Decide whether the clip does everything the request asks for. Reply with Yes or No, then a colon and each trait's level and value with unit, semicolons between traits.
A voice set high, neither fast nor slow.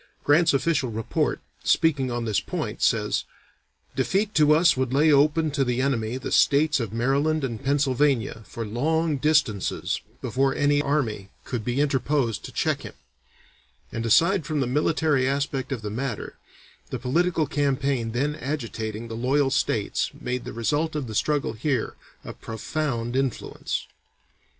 No: low, 135 Hz; average, 150 wpm